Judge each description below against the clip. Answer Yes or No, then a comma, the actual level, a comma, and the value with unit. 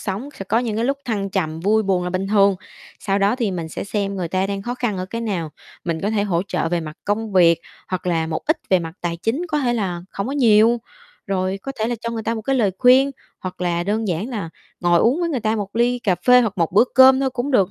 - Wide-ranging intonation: No, average, 4.4 semitones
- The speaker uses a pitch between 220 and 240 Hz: No, high, 205 Hz